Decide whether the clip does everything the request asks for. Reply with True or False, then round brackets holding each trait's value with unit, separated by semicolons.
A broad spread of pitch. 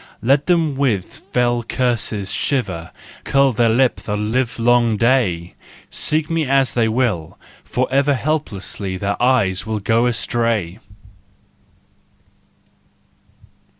False (4.2 semitones)